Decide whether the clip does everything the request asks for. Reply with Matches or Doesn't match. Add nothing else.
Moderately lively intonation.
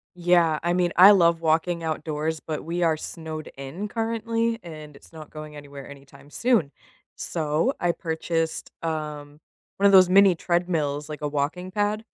Matches